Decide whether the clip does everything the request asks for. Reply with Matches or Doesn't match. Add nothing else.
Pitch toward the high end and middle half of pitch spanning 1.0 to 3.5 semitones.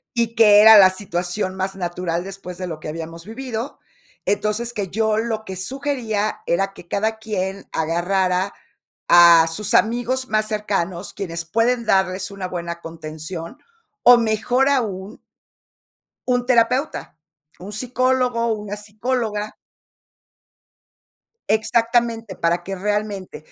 Doesn't match